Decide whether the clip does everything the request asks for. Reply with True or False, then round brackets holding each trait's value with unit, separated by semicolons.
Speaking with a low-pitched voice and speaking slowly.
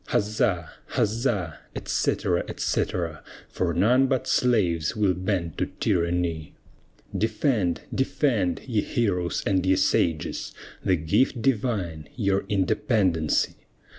True (95 Hz; 105 wpm)